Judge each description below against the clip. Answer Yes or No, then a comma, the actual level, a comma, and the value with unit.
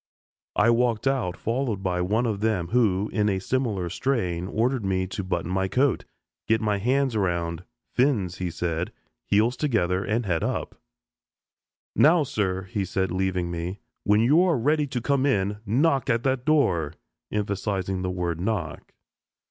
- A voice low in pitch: Yes, low, 105 Hz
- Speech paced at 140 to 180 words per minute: Yes, average, 160 wpm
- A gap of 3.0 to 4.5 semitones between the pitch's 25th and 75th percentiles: No, average, 5.1 semitones